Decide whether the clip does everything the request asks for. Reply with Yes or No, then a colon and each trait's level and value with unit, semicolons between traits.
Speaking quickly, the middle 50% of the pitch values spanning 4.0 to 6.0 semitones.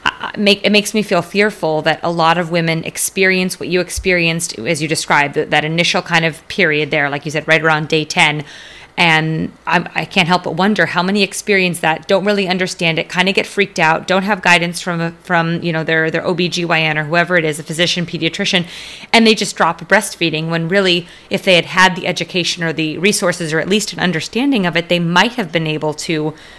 No: fast, 220 wpm; average, 2.7 semitones